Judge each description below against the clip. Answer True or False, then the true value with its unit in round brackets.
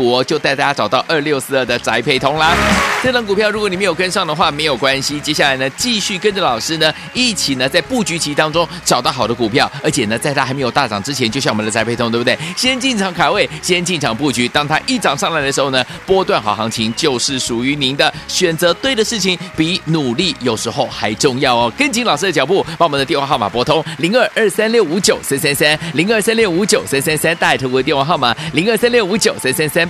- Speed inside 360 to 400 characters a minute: True (365 characters per minute)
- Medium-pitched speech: True (155 Hz)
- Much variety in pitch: True (6.2 semitones)